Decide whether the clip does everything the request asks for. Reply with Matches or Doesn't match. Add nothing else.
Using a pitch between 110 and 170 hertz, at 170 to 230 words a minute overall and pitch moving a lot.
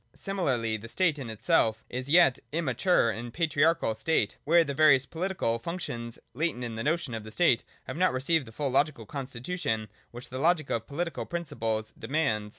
Matches